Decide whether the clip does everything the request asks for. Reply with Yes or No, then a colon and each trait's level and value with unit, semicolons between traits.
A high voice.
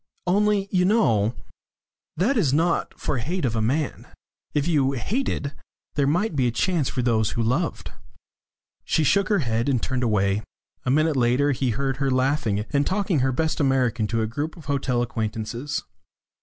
No: low, 135 Hz